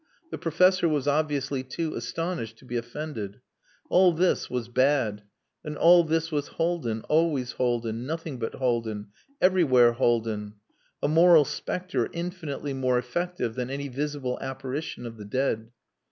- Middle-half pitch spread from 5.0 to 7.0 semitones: Yes, average, 5.3 semitones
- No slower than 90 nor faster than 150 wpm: Yes, average, 140 wpm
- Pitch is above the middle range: No, low, 135 Hz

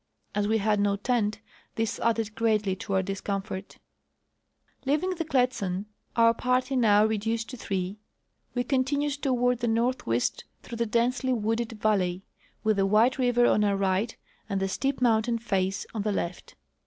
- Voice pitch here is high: Yes, high, 225 Hz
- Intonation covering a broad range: No, average, 3.5 semitones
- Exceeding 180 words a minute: No, average, 165 wpm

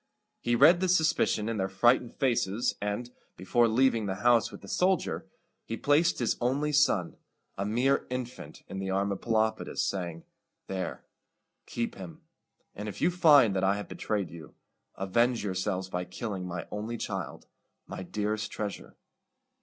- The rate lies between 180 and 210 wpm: No, average, 160 wpm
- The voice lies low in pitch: Yes, low, 110 Hz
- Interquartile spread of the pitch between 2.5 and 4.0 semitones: No, average, 4.4 semitones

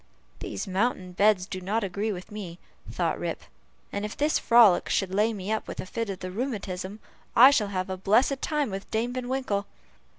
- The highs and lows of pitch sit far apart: No, average, 3.6 semitones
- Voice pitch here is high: Yes, high, 205 Hz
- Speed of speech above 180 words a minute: Yes, average, 200 wpm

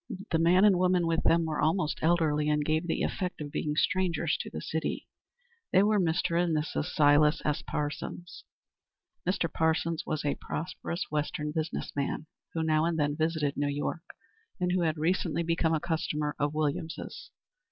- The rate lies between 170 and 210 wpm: Yes, average, 175 wpm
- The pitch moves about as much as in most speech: No, narrow, 2.2 semitones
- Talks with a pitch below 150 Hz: No, medium, 160 Hz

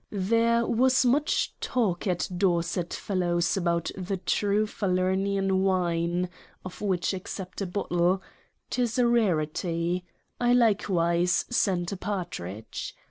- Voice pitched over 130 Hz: Yes, medium, 185 Hz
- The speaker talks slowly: Yes, slow, 115 wpm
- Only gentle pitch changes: No, average, 3.2 semitones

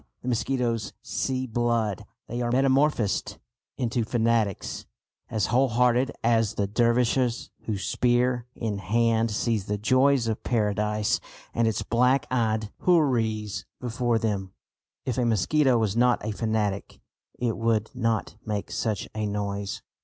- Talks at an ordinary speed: No, slow, 130 wpm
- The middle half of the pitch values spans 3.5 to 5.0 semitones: No, narrow, 2.5 semitones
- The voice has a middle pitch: No, low, 115 Hz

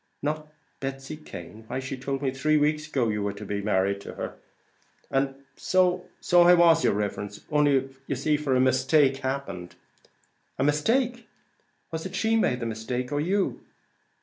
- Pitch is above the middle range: No, low, 135 Hz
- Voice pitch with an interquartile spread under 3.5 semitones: No, average, 3.8 semitones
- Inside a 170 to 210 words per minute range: Yes, average, 175 wpm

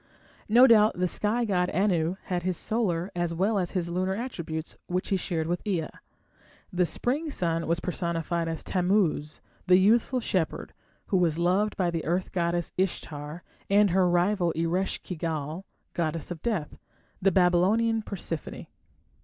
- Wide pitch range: No, average, 2.9 semitones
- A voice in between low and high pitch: Yes, medium, 180 Hz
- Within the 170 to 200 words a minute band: No, average, 155 wpm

